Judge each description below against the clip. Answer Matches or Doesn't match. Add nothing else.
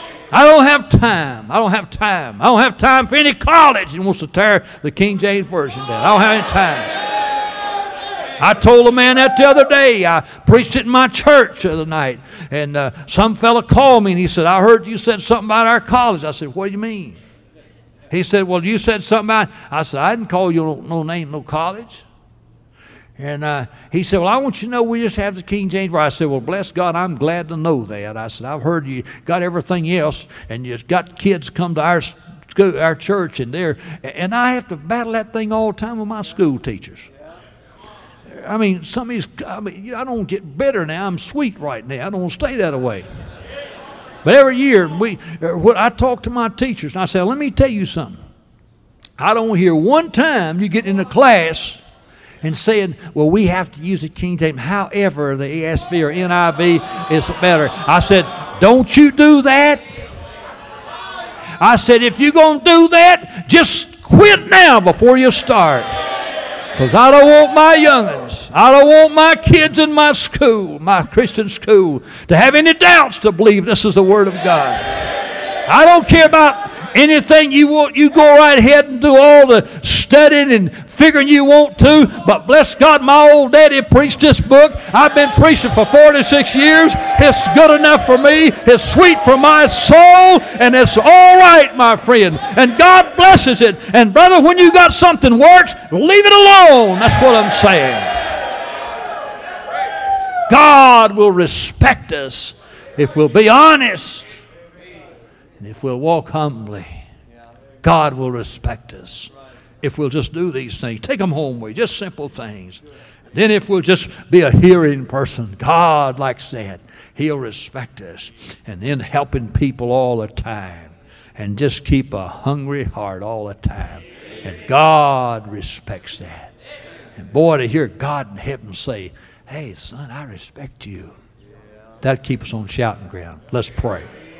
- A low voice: Doesn't match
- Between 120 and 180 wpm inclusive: Doesn't match